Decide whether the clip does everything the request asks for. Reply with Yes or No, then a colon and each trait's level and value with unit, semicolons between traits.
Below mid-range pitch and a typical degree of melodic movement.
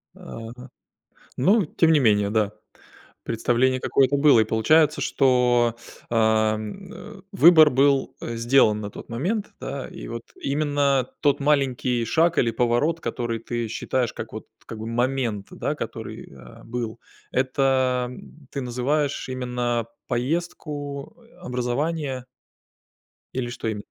Yes: low, 125 Hz; average, 3.5 semitones